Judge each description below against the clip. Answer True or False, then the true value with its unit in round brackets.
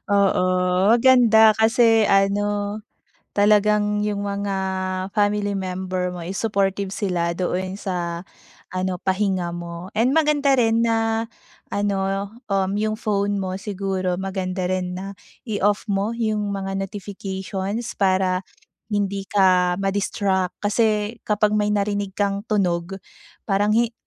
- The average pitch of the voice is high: True (200 Hz)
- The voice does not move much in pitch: True (1.9 semitones)